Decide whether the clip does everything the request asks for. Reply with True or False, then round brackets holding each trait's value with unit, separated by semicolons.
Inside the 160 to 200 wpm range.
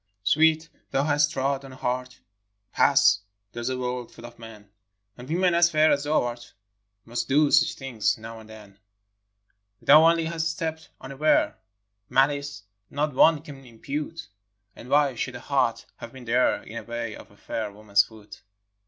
True (180 wpm)